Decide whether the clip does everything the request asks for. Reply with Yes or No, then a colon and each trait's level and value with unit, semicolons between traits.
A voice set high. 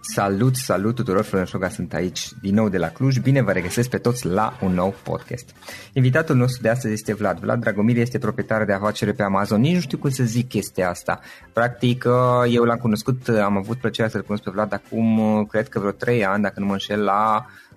No: low, 110 Hz